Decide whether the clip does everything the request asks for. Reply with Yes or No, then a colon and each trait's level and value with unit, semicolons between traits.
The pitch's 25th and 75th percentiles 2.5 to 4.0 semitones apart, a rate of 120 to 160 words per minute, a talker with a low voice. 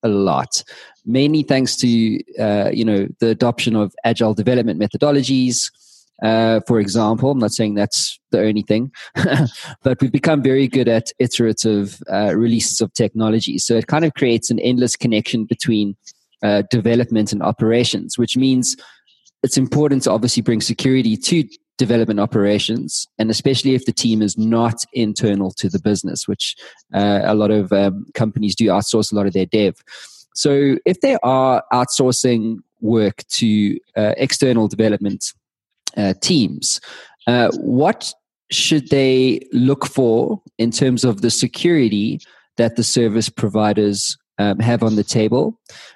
Yes: average, 3.1 semitones; average, 150 wpm; low, 115 Hz